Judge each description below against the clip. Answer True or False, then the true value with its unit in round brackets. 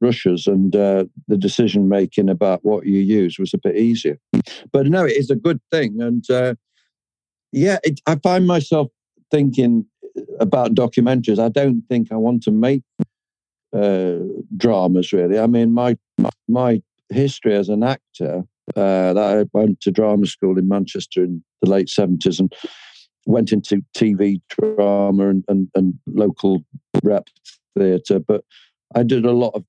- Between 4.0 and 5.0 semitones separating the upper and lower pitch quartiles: True (4.5 semitones)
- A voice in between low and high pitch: False (105 Hz)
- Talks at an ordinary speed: True (160 wpm)